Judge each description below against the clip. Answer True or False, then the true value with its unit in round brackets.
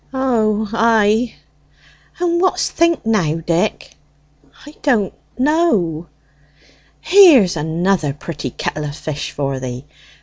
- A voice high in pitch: True (210 Hz)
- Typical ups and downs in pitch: False (8.7 semitones)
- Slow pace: True (105 wpm)